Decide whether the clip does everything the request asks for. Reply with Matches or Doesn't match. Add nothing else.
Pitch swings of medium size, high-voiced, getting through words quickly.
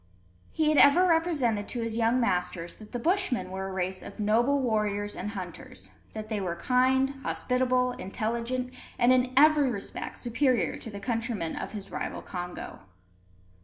Doesn't match